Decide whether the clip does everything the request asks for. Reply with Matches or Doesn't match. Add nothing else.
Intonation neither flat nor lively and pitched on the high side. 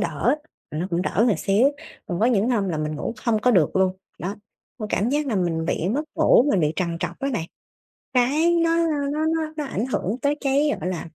Doesn't match